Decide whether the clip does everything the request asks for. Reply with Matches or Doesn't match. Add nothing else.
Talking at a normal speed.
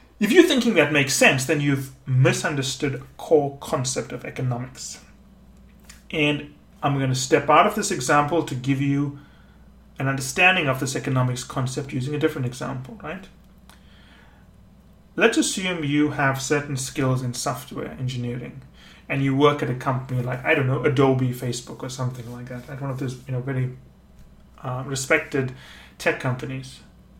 Matches